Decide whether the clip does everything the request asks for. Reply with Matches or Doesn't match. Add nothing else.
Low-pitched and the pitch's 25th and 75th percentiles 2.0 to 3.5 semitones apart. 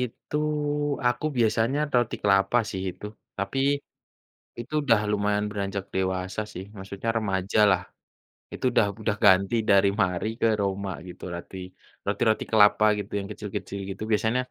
Matches